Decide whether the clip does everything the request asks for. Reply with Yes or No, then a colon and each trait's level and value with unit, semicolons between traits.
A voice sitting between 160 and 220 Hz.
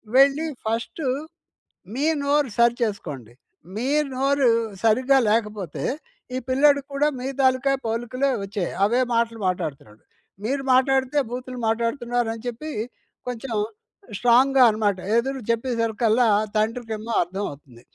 No: high, 235 Hz